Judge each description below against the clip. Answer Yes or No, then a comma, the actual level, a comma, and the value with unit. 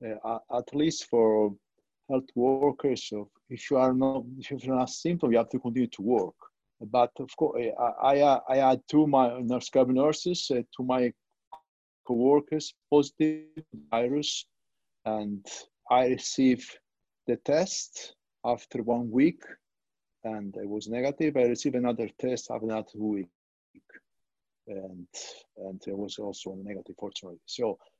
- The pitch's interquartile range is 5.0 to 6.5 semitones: No, average, 3.7 semitones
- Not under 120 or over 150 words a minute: Yes, average, 140 wpm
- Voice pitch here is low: Yes, low, 125 Hz